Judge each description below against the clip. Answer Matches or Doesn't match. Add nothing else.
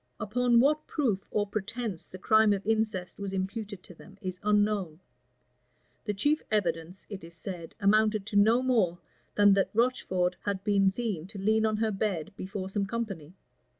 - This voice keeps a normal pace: Matches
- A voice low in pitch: Doesn't match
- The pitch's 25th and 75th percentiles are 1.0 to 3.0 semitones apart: Matches